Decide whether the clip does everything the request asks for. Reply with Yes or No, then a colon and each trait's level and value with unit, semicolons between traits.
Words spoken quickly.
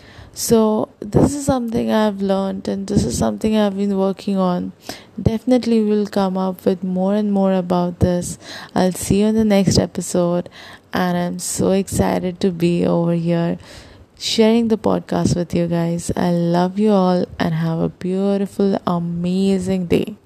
No: average, 165 wpm